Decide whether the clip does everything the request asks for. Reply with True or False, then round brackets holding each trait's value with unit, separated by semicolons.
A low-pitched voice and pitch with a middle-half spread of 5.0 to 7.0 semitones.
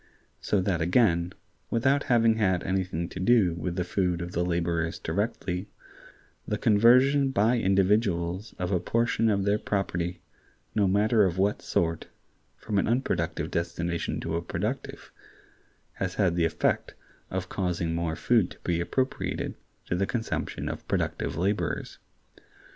False (95 Hz; 4.0 semitones)